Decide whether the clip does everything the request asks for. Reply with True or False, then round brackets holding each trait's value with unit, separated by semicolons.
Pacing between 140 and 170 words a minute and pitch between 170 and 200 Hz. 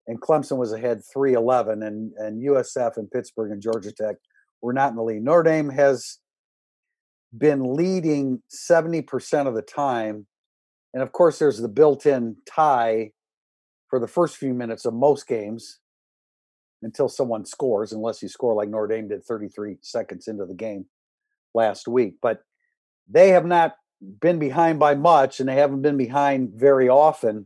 False (160 wpm; 130 Hz)